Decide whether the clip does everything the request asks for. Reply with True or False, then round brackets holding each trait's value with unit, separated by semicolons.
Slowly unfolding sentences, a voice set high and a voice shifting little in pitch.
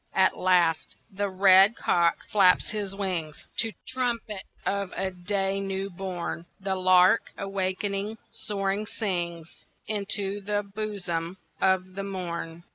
True (120 wpm; 195 Hz; 1.7 semitones)